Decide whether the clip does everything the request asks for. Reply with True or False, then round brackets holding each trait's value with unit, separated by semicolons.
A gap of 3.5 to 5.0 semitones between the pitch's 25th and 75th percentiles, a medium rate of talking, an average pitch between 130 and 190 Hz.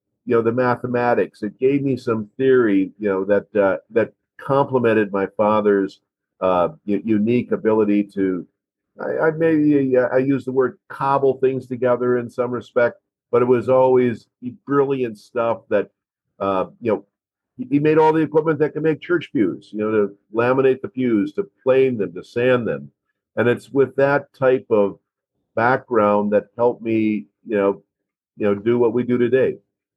False (4.1 semitones; 175 wpm; 120 Hz)